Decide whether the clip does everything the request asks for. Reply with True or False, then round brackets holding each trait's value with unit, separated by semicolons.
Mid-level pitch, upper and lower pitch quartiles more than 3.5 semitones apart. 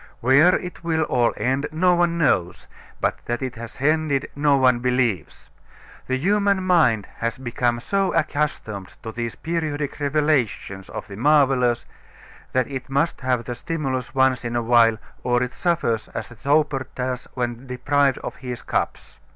False (130 Hz; 4.1 semitones)